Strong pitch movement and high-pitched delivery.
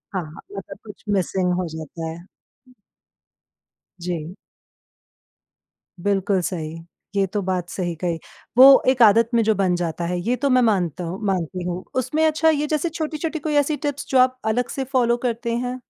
Yes: wide, 6.5 semitones; high, 210 Hz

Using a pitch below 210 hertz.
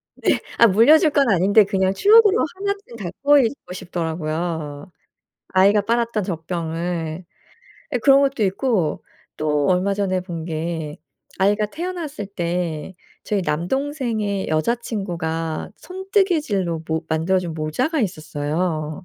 Yes: high, 190 Hz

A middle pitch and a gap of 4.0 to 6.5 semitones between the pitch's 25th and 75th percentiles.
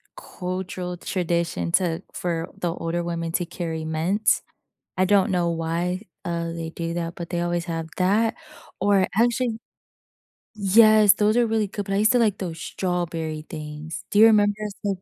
No: medium, 180 Hz; average, 3.5 semitones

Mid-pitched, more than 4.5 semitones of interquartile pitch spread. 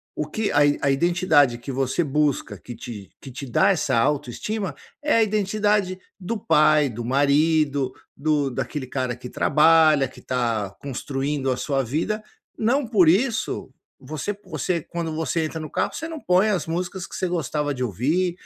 Yes: medium, 155 Hz; wide, 5.4 semitones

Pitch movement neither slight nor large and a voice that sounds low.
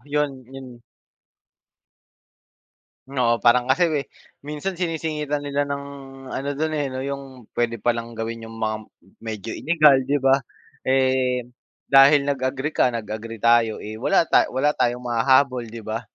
Yes: average, 3.4 semitones; low, 130 Hz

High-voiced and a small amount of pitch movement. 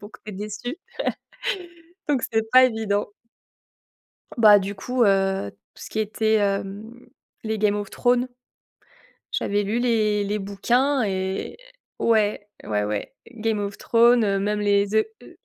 Yes: high, 210 Hz; narrow, 2.2 semitones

